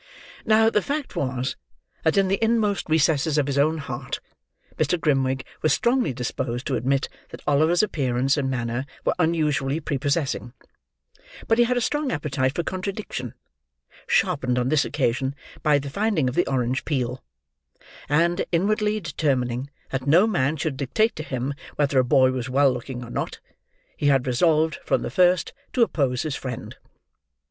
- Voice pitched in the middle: Yes, medium, 145 Hz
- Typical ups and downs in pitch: Yes, average, 4.8 semitones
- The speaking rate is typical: Yes, average, 165 wpm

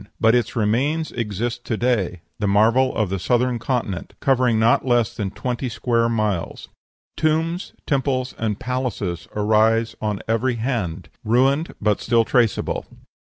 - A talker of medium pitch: No, low, 115 Hz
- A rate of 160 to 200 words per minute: No, average, 140 wpm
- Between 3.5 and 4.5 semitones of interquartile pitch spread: No, average, 3.1 semitones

